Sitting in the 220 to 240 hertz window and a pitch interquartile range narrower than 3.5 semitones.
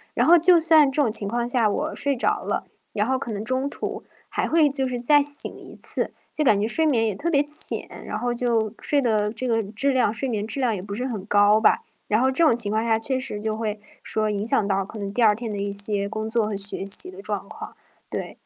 No: high, 225 Hz; average, 4.1 semitones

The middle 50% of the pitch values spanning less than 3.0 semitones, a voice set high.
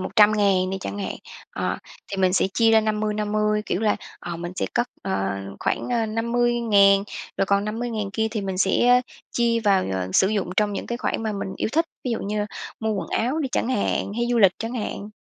Yes: narrow, 2.6 semitones; high, 210 Hz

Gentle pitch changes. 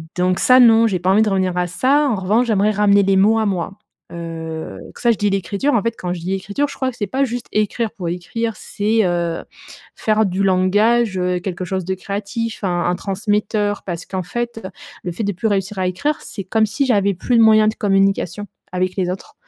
No: average, 3.3 semitones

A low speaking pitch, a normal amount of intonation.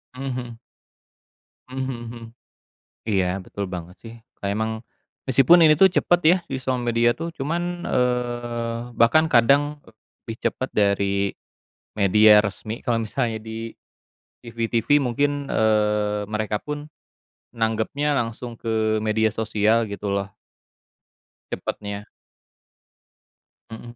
Yes: low, 115 Hz; average, 3.2 semitones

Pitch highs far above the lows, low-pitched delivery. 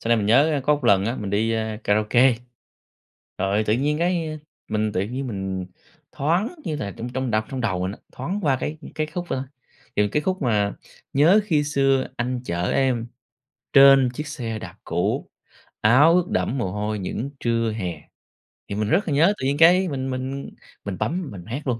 Yes: wide, 5.8 semitones; low, 130 Hz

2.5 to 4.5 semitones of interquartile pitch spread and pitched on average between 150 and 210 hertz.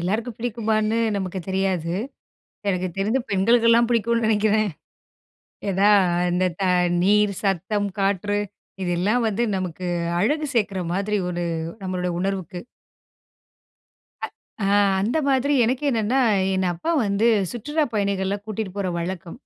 Yes: average, 3.4 semitones; high, 205 Hz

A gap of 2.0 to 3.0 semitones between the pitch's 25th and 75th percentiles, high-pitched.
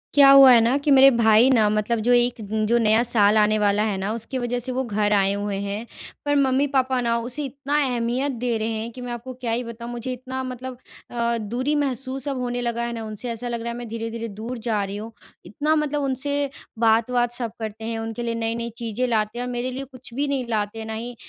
Yes: narrow, 2.6 semitones; high, 235 Hz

